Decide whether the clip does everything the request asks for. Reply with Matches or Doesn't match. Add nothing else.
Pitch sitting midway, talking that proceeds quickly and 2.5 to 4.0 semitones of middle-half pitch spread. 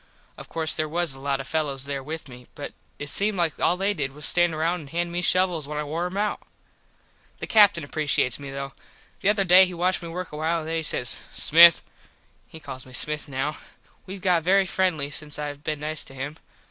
Matches